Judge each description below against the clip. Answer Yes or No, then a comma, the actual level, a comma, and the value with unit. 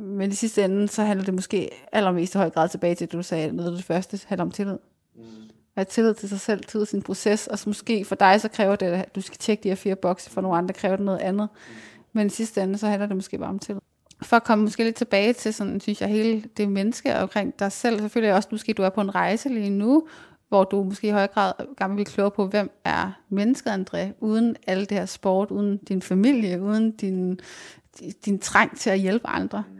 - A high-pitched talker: Yes, high, 200 Hz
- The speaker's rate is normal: No, fast, 255 wpm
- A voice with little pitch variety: Yes, narrow, 2.1 semitones